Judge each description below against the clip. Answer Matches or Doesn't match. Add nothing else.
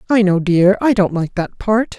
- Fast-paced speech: Matches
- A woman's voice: Matches